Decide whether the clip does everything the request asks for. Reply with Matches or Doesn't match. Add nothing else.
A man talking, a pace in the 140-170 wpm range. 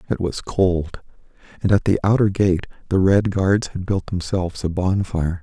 Doesn't match